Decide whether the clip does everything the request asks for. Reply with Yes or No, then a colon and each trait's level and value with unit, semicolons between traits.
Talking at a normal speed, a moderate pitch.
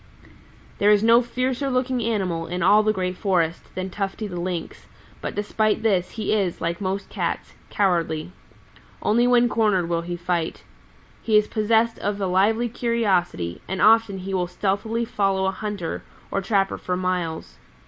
No: average, 165 wpm; high, 195 Hz